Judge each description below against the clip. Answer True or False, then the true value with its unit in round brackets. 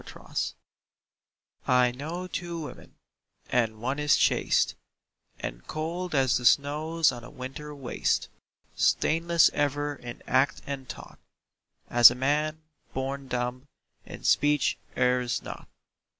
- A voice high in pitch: False (140 Hz)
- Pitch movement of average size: True (3.4 semitones)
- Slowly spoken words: True (125 wpm)